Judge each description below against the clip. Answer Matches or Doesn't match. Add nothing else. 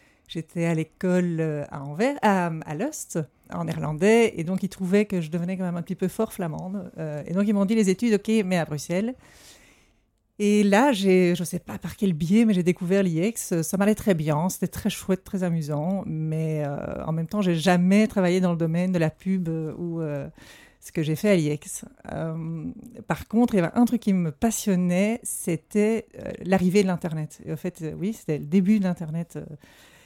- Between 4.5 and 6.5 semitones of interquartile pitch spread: Doesn't match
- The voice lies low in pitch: Doesn't match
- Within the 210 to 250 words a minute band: Matches